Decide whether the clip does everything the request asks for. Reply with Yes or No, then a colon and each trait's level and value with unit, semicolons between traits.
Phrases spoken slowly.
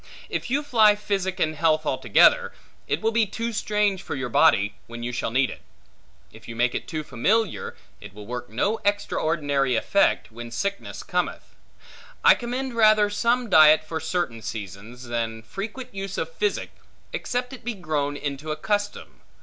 No: average, 170 wpm